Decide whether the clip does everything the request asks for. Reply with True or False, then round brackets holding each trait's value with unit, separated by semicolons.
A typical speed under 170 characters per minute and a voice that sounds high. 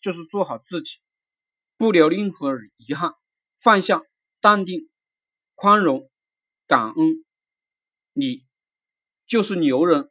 True (150 characters per minute; 270 Hz)